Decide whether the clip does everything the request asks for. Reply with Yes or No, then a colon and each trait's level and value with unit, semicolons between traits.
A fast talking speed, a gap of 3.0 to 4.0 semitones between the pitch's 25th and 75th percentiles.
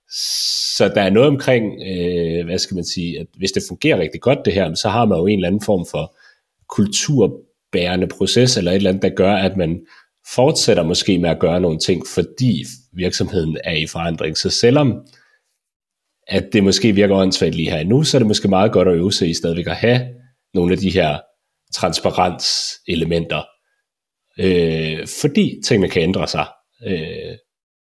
No: average, 180 wpm; average, 3.6 semitones